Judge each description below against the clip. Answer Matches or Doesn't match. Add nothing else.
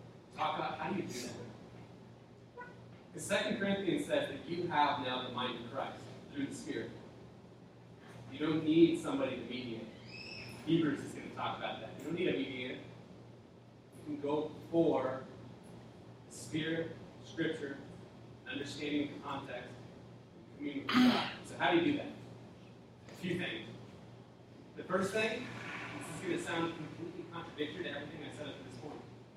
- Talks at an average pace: Matches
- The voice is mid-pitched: Matches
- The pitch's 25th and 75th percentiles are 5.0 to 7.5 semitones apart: Matches